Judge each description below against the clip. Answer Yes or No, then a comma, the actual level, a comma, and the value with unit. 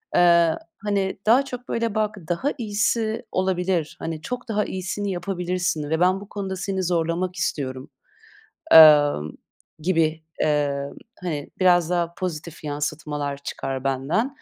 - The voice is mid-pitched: Yes, medium, 175 Hz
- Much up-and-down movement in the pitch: No, average, 4.4 semitones